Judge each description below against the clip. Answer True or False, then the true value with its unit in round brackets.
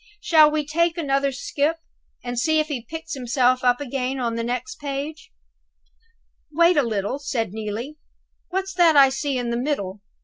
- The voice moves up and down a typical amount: True (4.0 semitones)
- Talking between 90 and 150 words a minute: False (170 wpm)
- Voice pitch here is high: True (275 Hz)